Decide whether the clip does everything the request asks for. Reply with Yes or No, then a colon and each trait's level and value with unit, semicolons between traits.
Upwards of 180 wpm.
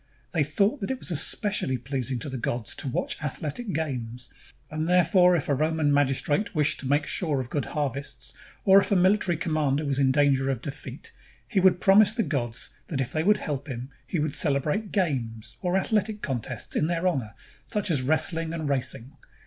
Yes: average, 195 wpm